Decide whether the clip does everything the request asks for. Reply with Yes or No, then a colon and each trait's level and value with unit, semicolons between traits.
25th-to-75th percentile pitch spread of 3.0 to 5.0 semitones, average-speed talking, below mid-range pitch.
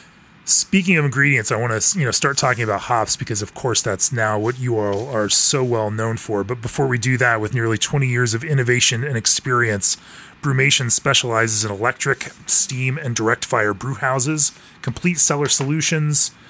Yes: average, 3.9 semitones; average, 185 wpm; low, 125 Hz